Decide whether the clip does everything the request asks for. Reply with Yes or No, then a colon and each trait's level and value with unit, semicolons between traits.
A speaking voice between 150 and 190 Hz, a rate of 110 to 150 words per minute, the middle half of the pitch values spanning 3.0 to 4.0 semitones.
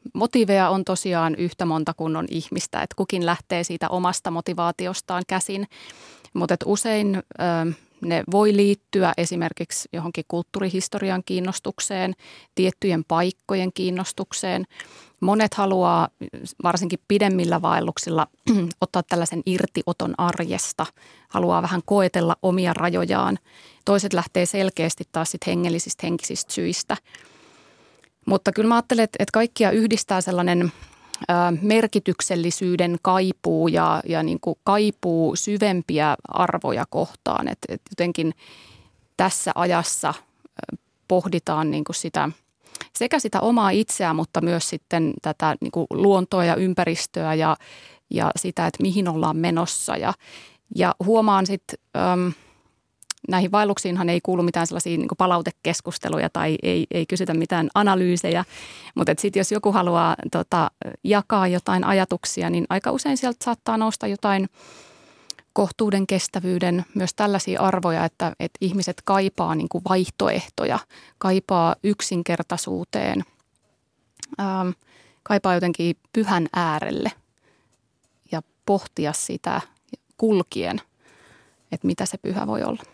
No: medium, 185 Hz; average, 115 wpm; narrow, 2.6 semitones